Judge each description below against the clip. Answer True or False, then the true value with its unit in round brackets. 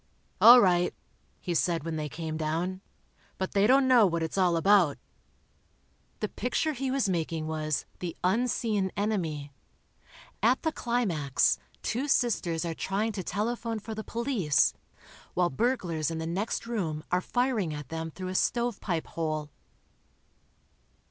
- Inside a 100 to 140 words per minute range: False (150 wpm)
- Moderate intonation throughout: False (6.0 semitones)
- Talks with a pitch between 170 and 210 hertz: True (185 Hz)